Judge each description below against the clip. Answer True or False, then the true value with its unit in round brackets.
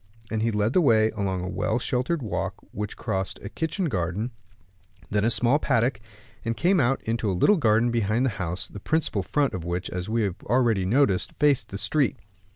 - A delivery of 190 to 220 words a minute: True (200 wpm)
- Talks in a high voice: False (110 Hz)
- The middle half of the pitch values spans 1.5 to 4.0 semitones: False (4.7 semitones)